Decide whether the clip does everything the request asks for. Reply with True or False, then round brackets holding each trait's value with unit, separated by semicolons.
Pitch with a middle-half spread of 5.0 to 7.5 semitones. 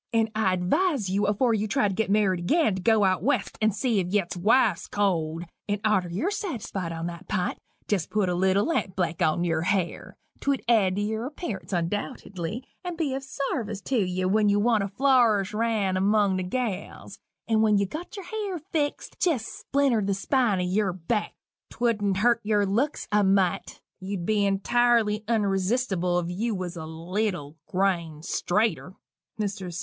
False (3.9 semitones)